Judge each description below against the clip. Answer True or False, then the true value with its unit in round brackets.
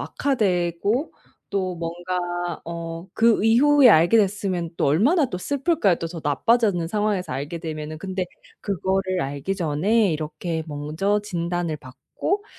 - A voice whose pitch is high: False (180 Hz)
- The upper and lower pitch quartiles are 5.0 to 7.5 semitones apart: False (4.0 semitones)